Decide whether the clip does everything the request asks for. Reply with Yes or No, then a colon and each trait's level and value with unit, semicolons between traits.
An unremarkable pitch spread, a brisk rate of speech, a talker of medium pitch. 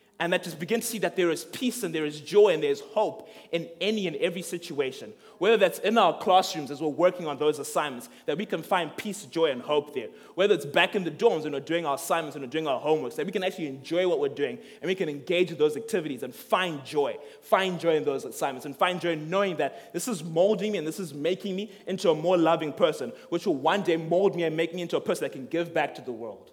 Yes: average, 3.9 semitones; fast, 275 wpm; medium, 175 Hz